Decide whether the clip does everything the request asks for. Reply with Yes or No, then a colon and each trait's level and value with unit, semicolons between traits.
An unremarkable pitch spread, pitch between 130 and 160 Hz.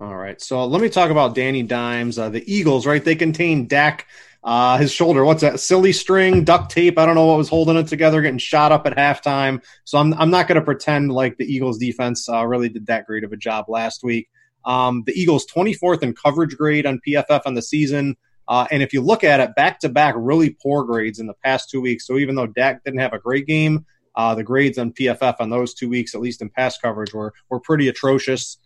Yes: average, 4.1 semitones; low, 135 Hz